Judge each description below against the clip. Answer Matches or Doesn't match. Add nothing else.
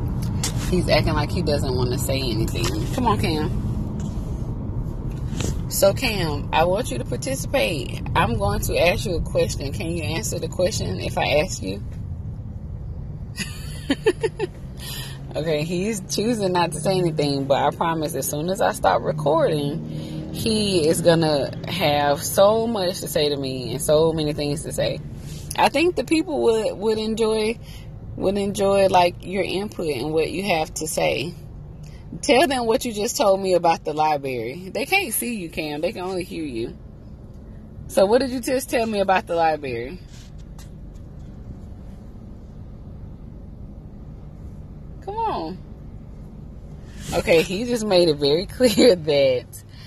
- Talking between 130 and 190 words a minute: Matches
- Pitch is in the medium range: Matches